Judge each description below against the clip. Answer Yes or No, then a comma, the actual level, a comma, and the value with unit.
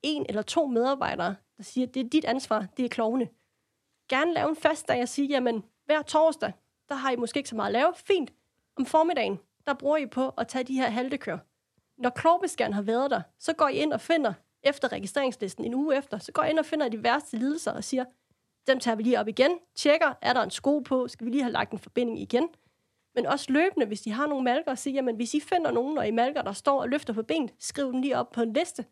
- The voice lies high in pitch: Yes, very high, 260 Hz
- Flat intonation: No, average, 4.0 semitones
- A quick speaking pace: Yes, fast, 255 wpm